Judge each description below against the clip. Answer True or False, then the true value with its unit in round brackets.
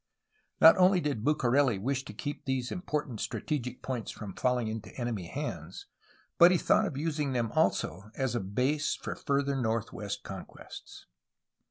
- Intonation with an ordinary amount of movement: True (4.6 semitones)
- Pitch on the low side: True (130 Hz)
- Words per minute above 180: False (160 wpm)